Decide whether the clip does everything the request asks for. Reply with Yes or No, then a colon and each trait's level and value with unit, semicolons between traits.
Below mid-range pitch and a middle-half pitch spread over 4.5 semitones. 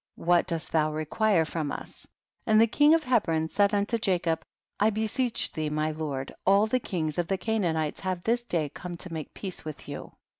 No: medium, 175 Hz; wide, 5.5 semitones